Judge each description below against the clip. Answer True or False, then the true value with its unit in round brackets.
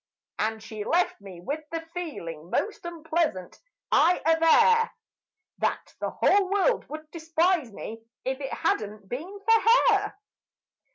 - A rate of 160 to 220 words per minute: False (135 wpm)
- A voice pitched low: False (320 Hz)